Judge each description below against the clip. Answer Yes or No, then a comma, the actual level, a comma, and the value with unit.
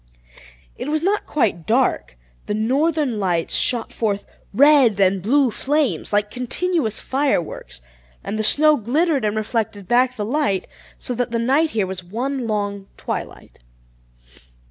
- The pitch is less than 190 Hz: No, high, 235 Hz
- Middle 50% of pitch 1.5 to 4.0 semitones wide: No, wide, 5.6 semitones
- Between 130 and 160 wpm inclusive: Yes, average, 145 wpm